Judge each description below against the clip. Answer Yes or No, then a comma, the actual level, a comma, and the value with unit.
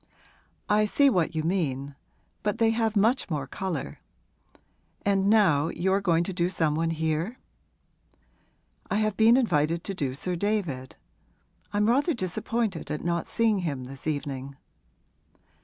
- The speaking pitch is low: No, medium, 180 Hz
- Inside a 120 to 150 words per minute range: Yes, average, 145 wpm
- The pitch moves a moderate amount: No, wide, 5.7 semitones